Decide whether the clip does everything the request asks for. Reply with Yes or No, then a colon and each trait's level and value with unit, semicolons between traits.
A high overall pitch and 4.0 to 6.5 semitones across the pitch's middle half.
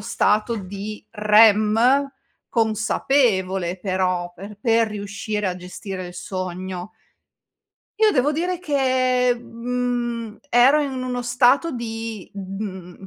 Yes: high, 220 Hz; average, 4.4 semitones